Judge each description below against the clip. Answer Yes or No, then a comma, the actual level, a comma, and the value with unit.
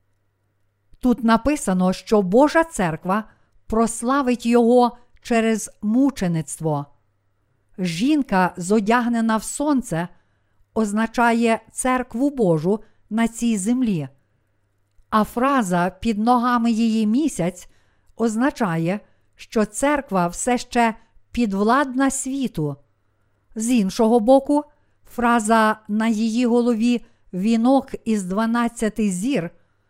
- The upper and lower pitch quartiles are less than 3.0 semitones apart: No, average, 5.3 semitones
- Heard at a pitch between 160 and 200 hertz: No, high, 225 Hz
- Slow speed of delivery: Yes, slow, 85 wpm